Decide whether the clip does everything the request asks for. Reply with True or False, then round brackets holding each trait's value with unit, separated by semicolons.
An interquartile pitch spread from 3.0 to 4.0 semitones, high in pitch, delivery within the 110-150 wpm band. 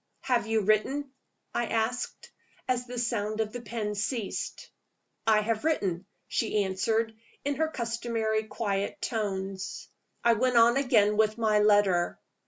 False (2.4 semitones; 220 Hz; 140 wpm)